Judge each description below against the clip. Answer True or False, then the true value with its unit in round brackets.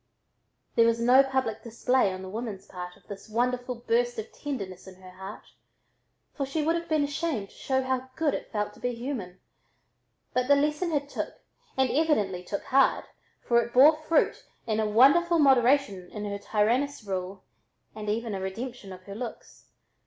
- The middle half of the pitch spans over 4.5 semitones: True (5.2 semitones)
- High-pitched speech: True (235 Hz)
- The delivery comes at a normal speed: True (180 wpm)